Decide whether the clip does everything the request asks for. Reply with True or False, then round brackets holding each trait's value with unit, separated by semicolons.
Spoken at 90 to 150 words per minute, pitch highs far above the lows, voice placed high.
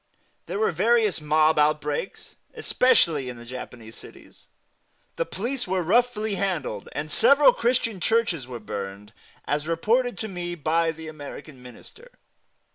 False (135 wpm; 7.4 semitones; 165 Hz)